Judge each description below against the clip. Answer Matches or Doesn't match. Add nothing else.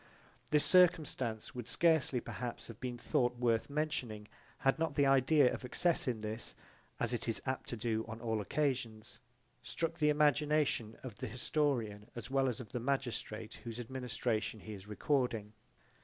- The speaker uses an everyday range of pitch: Matches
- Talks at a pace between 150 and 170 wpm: Matches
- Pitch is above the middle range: Doesn't match